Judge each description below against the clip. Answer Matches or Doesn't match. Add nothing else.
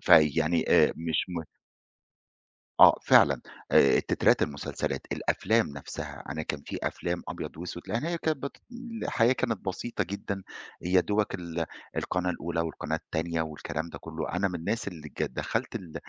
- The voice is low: Matches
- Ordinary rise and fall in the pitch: Matches